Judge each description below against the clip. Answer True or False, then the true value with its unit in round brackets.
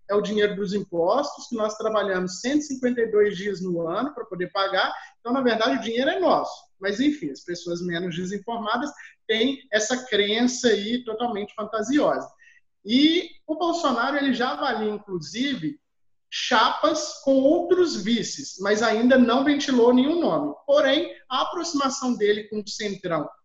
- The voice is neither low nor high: False (240 Hz)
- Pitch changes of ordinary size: False (5.8 semitones)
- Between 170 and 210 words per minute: False (150 wpm)